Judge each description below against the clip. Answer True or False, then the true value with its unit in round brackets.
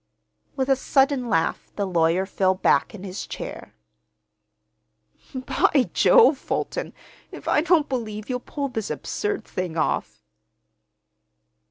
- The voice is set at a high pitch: True (245 Hz)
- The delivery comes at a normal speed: False (125 wpm)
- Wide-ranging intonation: True (6.7 semitones)